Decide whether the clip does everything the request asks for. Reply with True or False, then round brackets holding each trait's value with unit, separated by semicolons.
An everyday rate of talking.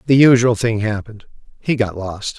True (175 wpm)